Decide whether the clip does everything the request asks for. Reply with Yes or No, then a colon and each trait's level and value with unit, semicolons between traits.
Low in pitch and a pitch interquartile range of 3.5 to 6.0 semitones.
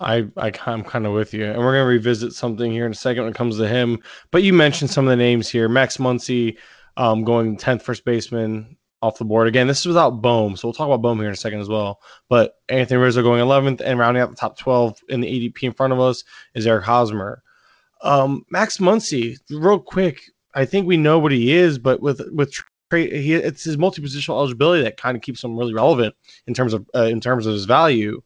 No: low, 125 Hz; average, 3.1 semitones